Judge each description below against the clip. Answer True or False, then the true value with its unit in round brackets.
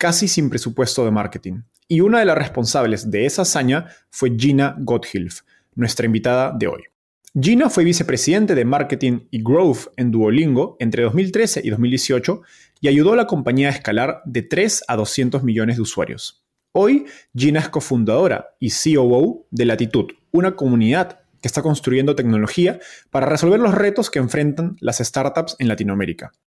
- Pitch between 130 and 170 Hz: True (135 Hz)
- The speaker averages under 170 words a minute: True (160 wpm)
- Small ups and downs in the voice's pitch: False (5.2 semitones)